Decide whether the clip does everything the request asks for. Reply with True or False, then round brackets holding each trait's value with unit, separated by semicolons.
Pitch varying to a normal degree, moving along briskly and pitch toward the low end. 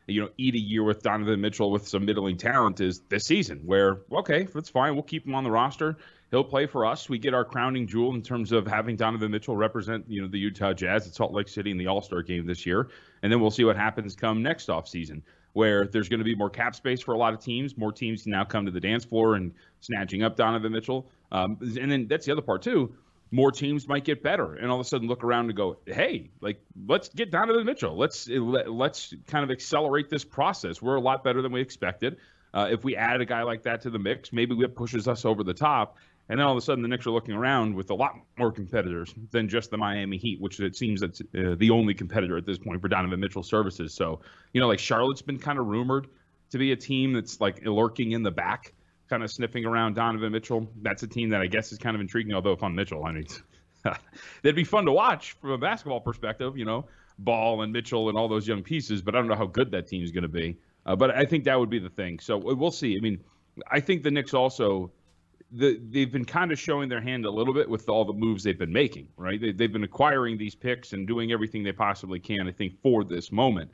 True (4.2 semitones; 255 wpm; 115 Hz)